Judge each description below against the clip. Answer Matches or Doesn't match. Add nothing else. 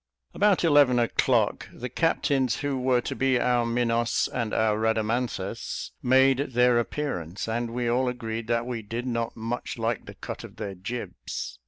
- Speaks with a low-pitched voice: Matches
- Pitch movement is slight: Matches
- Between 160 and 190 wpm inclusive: Matches